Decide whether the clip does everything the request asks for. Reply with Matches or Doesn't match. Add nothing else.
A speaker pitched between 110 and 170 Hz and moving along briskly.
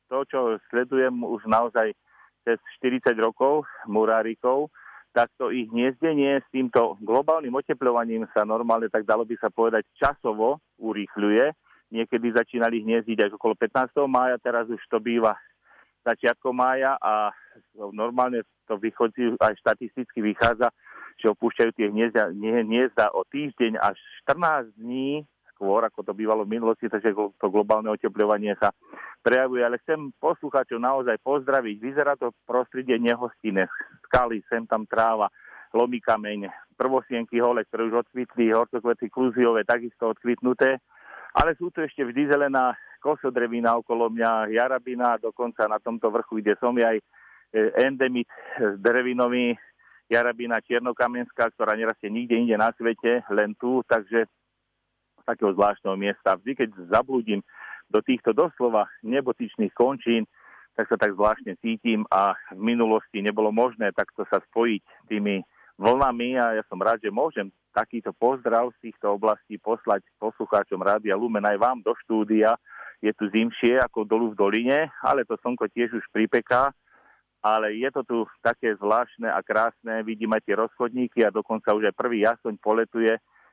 Doesn't match